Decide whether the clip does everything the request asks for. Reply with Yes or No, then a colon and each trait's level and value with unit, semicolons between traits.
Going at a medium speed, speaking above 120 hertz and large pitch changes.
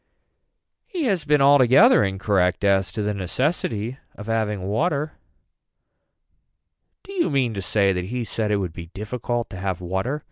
No: average, 155 wpm; low, 110 Hz; wide, 6.0 semitones